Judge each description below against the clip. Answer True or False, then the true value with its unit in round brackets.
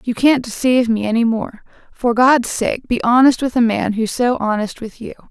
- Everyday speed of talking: False (215 wpm)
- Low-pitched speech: False (235 Hz)